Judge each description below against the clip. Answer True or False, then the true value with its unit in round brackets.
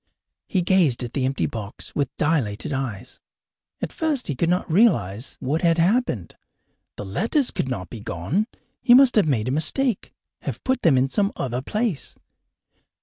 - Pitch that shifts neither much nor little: False (8.9 semitones)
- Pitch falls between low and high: True (150 Hz)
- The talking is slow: False (170 wpm)